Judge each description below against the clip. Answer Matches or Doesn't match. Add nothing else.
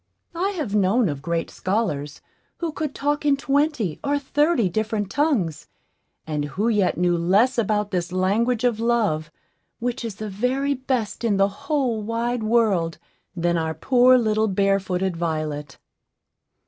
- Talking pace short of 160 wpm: Matches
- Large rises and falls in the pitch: Matches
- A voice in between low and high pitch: Doesn't match